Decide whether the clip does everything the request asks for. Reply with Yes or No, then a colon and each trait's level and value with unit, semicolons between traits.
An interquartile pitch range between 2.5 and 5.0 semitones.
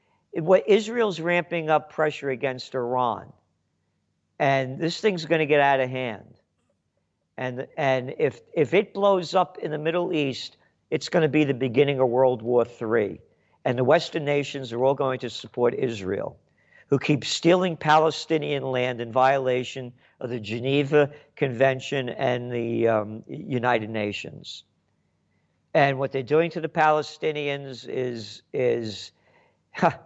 Yes: average, 3.8 semitones